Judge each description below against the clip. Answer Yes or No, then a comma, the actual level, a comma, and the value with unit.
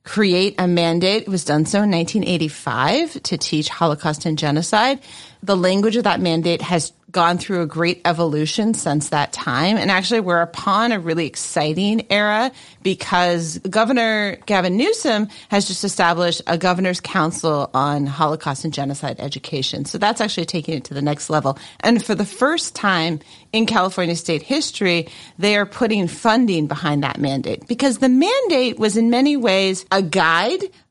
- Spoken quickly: No, average, 165 wpm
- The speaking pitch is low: No, medium, 180 Hz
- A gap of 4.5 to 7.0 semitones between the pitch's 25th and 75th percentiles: Yes, average, 5.0 semitones